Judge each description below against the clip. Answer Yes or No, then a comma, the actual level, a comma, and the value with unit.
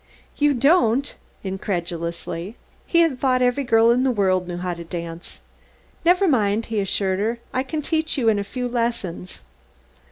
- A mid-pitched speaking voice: No, high, 225 Hz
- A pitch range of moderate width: No, wide, 5.8 semitones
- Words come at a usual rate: Yes, average, 165 wpm